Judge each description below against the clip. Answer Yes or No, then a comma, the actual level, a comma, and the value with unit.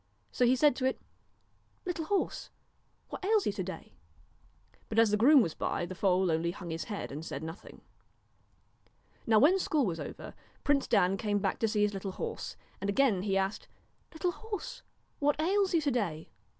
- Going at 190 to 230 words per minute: Yes, average, 200 wpm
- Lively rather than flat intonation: Yes, wide, 8.1 semitones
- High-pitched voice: Yes, high, 215 Hz